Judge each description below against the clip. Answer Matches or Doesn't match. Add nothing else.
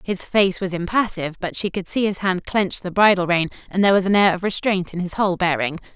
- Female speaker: Matches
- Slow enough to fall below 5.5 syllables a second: Doesn't match